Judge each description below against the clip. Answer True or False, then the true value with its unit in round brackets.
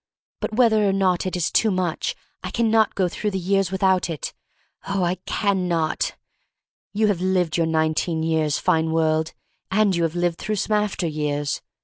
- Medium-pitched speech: True (180 Hz)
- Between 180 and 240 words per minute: True (195 wpm)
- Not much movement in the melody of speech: False (3.5 semitones)